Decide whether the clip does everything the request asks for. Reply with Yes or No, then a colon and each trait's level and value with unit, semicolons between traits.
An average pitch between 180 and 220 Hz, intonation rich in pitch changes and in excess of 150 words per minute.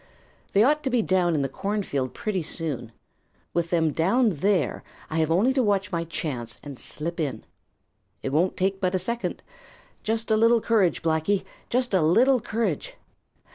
Yes: medium, 185 Hz; wide, 5.7 semitones; average, 175 wpm